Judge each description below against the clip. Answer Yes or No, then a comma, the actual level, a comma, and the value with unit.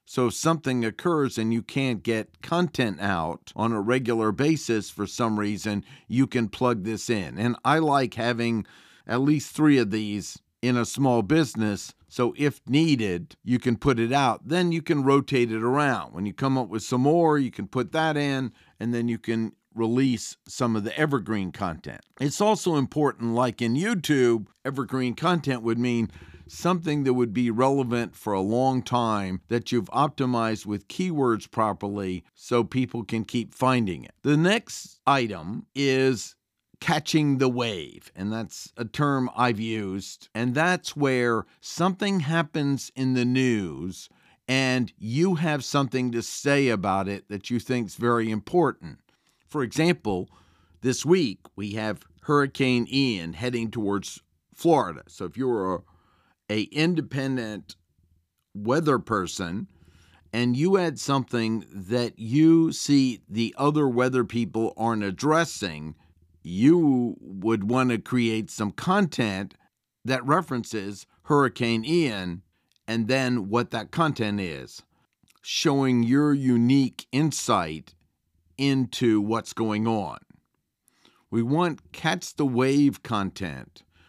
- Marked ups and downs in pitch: No, average, 4.5 semitones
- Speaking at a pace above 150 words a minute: No, average, 145 wpm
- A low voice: Yes, low, 120 Hz